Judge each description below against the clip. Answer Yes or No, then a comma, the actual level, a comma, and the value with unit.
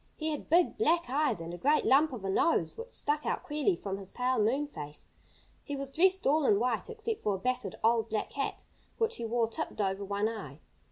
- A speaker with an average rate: No, fast, 225 wpm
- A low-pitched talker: No, very high, 255 Hz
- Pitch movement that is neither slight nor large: No, wide, 6.7 semitones